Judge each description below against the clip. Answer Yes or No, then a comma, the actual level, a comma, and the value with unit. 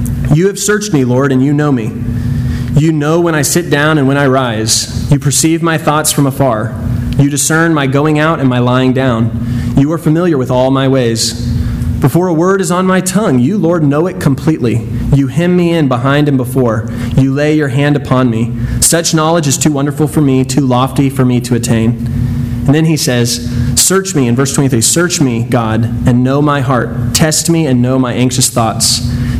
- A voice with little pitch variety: No, average, 4.2 semitones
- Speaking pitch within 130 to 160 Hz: Yes, low, 135 Hz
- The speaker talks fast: Yes, fast, 210 wpm